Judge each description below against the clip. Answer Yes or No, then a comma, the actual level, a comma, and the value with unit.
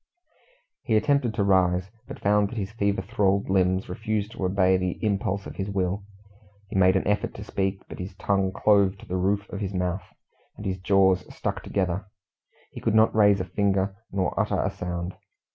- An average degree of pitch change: No, narrow, 1.6 semitones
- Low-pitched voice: Yes, very low, 95 Hz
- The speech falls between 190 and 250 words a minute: Yes, average, 195 wpm